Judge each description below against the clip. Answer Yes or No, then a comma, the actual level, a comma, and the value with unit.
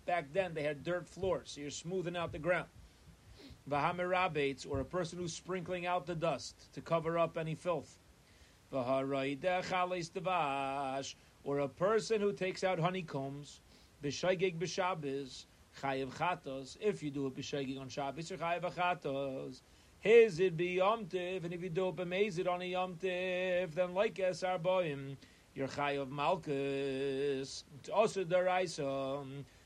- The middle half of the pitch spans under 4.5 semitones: No, average, 5.0 semitones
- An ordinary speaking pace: No, slow, 130 wpm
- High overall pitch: No, medium, 165 Hz